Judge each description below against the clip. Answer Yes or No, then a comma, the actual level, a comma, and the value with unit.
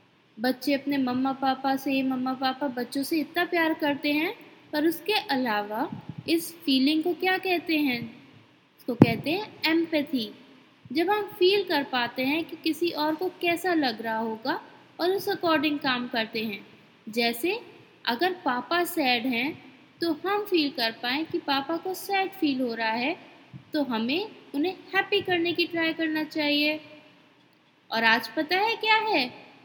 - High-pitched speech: Yes, very high, 310 Hz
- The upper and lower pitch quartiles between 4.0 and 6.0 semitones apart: Yes, average, 4.7 semitones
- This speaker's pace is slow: No, average, 160 wpm